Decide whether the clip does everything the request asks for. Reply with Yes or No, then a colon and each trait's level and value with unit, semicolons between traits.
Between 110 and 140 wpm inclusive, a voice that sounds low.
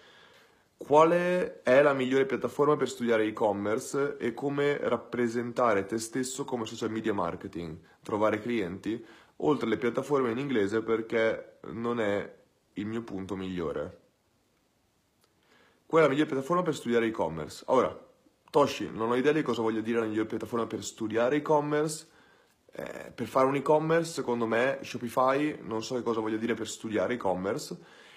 No: average, 150 wpm; low, 120 Hz